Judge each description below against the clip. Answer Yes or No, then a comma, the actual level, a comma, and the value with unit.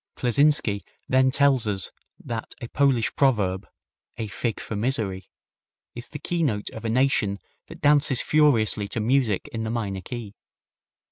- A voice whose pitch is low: Yes, low, 115 Hz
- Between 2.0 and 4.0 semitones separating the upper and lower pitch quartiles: No, average, 4.4 semitones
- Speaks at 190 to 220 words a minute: No, average, 145 wpm